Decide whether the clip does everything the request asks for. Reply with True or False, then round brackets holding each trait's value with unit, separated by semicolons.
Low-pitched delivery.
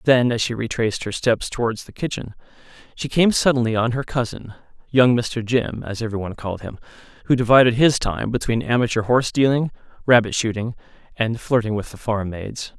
True (120 Hz)